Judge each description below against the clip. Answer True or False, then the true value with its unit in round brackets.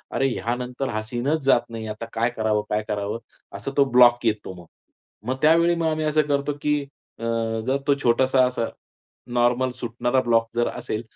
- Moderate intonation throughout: True (3.1 semitones)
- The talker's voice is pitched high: False (120 Hz)